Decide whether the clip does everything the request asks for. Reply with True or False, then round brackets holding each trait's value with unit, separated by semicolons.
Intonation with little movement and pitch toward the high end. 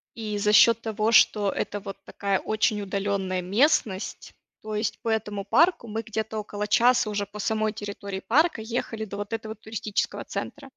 True (1.6 semitones; 215 Hz)